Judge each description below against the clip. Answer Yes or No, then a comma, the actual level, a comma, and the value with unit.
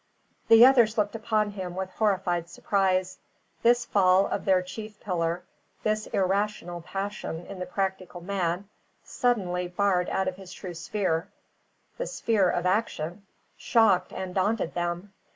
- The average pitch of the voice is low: No, high, 190 Hz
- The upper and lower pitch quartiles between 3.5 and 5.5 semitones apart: No, average, 2.8 semitones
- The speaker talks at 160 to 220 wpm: No, average, 140 wpm